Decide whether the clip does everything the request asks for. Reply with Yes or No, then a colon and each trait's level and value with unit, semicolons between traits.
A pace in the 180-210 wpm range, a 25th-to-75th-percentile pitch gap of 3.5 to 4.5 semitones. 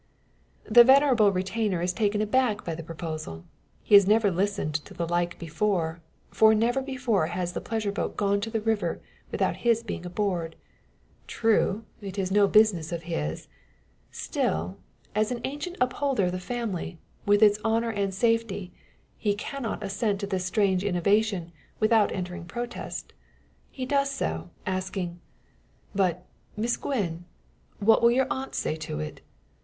No: average, 150 wpm; average, 4.1 semitones